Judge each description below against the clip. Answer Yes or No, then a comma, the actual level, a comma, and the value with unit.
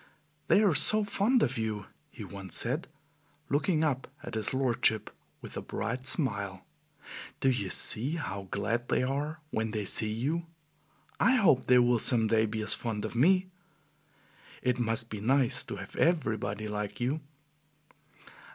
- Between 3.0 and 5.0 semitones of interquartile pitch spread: No, wide, 5.4 semitones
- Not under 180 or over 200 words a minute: No, average, 160 wpm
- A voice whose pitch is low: Yes, low, 120 Hz